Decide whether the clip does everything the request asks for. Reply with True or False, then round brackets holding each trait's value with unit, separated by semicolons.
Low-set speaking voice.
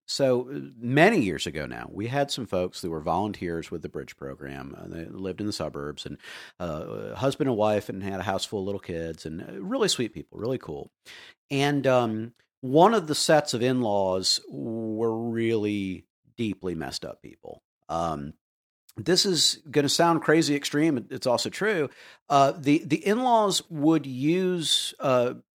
True (115 Hz)